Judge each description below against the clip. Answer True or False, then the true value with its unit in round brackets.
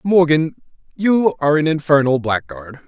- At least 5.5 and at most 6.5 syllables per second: False (4.9 syllables/s)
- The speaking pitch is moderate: True (150 Hz)